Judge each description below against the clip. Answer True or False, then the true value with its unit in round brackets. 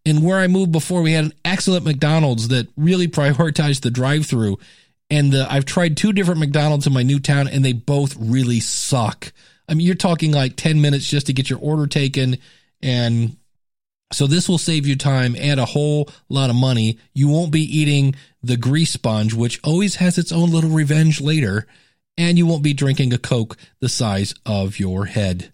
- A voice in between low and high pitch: True (145 Hz)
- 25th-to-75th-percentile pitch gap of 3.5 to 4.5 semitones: True (4.0 semitones)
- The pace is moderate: True (195 wpm)